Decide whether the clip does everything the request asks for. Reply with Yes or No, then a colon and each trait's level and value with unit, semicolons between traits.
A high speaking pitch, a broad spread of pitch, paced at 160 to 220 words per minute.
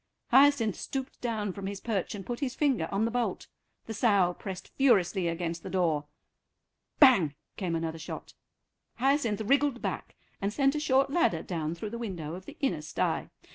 Yes: high, 205 Hz; wide, 6.8 semitones; average, 175 wpm